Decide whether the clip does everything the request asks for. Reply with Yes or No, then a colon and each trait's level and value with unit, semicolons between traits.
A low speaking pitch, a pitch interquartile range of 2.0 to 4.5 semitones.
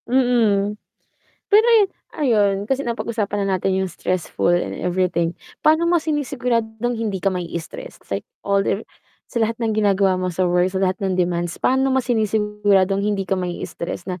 No: high, 200 Hz; average, 4.1 semitones